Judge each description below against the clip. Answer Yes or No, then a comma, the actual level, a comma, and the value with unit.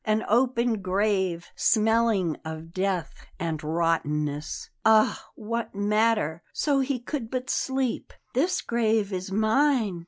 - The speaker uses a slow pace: Yes, slow, 120 wpm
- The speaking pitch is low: No, high, 215 Hz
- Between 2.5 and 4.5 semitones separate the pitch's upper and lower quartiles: No, average, 5.3 semitones